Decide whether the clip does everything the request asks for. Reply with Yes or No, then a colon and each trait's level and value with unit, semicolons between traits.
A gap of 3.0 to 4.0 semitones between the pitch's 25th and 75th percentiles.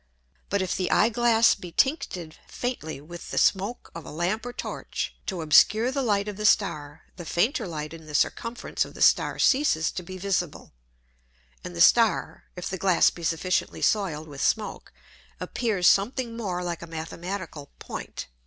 No: average, 5.1 semitones